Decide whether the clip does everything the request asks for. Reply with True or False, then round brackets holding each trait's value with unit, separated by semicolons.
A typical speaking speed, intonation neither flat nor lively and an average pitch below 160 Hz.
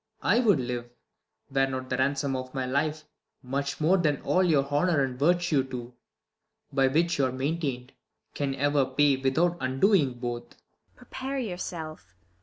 True (170 wpm; 3.9 semitones; 140 Hz)